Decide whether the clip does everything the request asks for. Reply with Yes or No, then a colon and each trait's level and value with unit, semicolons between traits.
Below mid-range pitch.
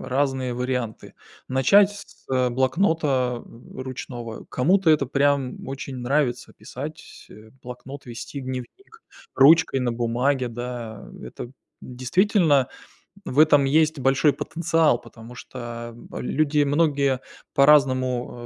Yes: low, 130 Hz